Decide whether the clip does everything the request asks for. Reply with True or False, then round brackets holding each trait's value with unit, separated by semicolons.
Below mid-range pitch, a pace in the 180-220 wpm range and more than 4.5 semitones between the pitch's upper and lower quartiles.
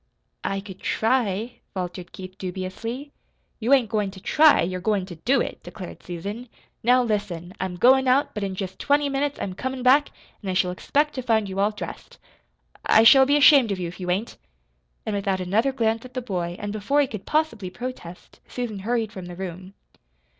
False (210 Hz; 200 wpm; 5.2 semitones)